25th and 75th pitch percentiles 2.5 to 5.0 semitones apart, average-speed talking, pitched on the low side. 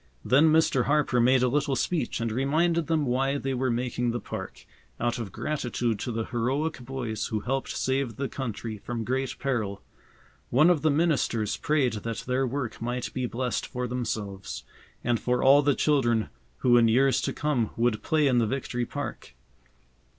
Yes: average, 2.9 semitones; average, 180 wpm; low, 125 Hz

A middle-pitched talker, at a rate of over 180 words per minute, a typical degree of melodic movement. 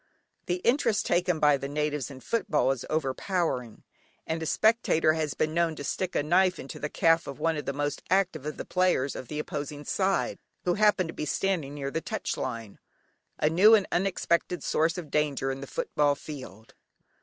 Yes: medium, 155 Hz; average, 195 wpm; average, 4.1 semitones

